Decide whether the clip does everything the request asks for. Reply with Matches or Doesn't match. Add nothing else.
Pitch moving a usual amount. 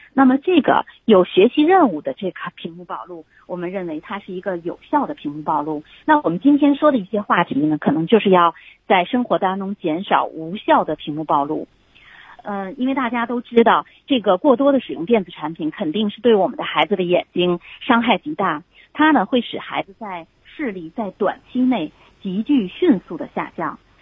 Doesn't match